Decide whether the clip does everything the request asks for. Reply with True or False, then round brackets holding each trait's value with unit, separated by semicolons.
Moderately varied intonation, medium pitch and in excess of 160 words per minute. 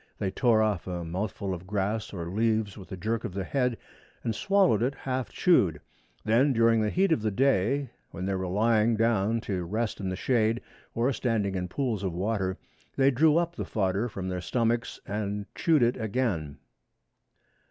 False (3.9 semitones; 110 Hz; 185 wpm)